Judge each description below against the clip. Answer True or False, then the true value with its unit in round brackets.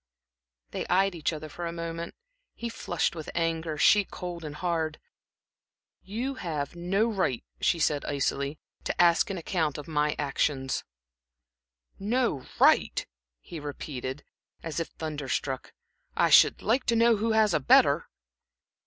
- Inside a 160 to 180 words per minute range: False (145 wpm)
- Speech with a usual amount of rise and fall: True (4.6 semitones)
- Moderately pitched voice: True (165 Hz)